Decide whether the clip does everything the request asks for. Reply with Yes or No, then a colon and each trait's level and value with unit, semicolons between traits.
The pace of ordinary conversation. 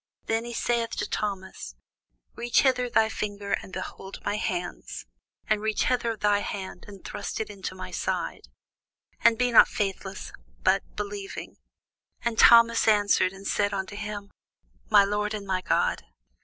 Yes: average, 155 wpm